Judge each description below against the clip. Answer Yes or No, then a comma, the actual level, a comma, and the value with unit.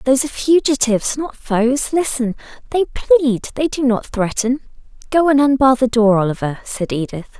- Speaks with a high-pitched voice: Yes, very high, 250 Hz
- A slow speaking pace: Yes, slow, 120 wpm